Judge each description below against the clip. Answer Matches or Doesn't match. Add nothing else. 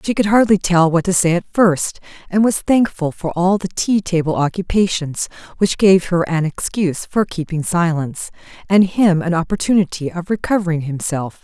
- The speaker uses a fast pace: Doesn't match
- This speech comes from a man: Doesn't match